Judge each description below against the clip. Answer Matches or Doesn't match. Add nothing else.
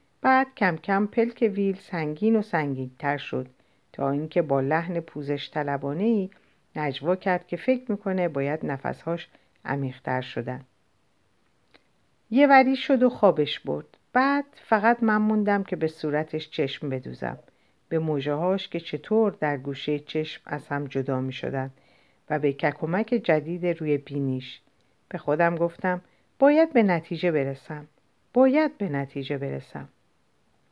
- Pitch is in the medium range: Matches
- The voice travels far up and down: Matches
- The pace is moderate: Matches